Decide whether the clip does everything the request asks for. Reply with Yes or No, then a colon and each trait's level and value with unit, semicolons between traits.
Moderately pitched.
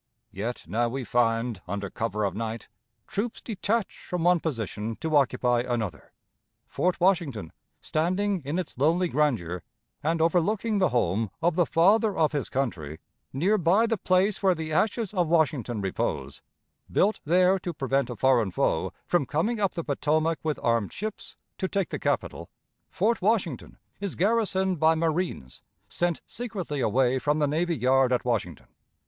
Yes: medium, 155 Hz